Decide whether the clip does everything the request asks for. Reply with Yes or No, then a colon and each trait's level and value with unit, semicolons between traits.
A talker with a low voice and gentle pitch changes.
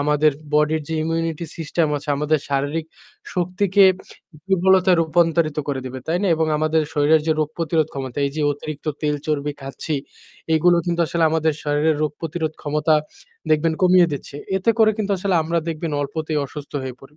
No: medium, 155 Hz; narrow, 2.3 semitones